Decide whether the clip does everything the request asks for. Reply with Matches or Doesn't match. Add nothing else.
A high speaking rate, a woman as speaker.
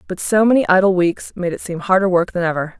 Matches